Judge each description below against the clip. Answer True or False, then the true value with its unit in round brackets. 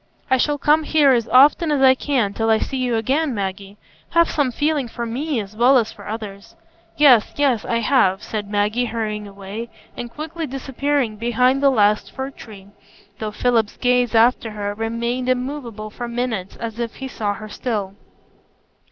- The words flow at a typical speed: True (180 wpm)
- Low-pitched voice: False (235 Hz)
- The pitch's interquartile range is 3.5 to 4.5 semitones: True (3.9 semitones)